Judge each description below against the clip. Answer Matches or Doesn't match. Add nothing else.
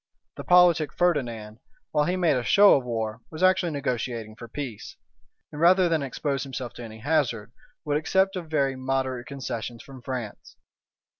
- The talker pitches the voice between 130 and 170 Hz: Matches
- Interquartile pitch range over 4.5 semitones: Matches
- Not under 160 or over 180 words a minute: Matches